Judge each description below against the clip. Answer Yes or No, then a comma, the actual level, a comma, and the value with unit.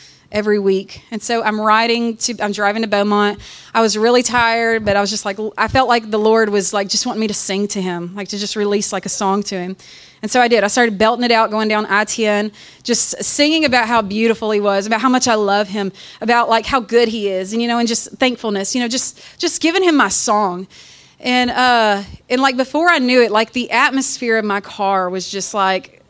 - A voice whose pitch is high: Yes, high, 220 Hz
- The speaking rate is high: Yes, fast, 240 wpm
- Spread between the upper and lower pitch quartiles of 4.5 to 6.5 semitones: No, average, 2.9 semitones